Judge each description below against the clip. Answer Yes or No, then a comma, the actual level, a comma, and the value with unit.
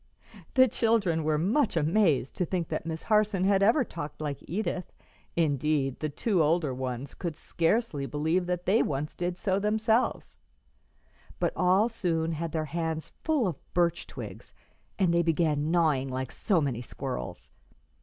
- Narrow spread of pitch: No, average, 4.3 semitones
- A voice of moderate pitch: Yes, medium, 170 Hz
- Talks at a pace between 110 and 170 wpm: Yes, average, 160 wpm